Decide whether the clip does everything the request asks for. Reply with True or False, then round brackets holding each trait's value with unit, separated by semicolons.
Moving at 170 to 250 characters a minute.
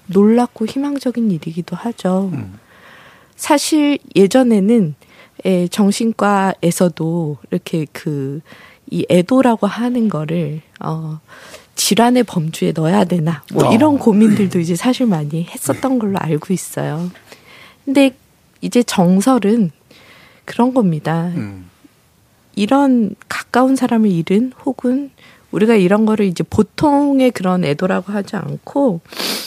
True (240 characters per minute)